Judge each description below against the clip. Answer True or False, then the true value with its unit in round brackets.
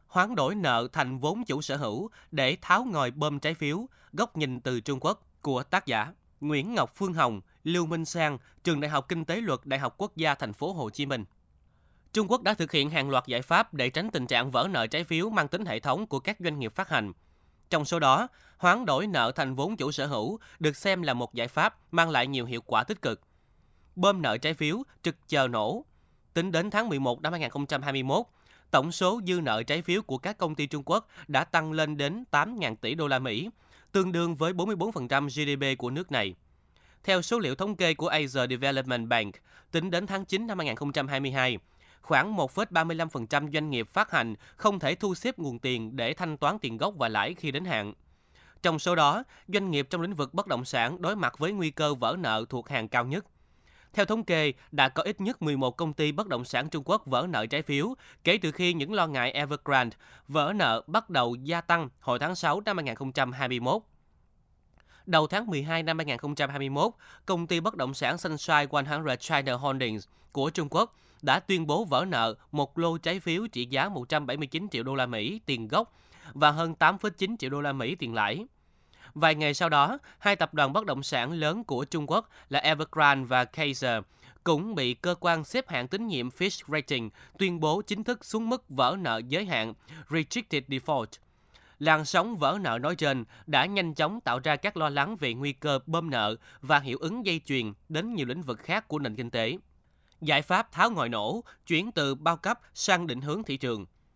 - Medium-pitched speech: True (150 Hz)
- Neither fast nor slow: True (210 wpm)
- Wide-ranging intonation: False (5.0 semitones)